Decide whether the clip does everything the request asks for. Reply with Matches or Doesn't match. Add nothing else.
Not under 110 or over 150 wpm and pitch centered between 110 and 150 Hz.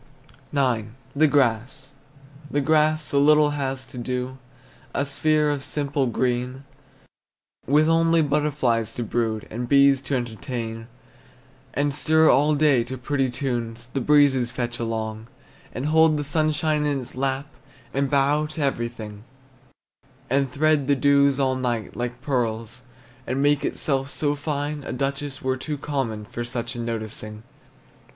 Matches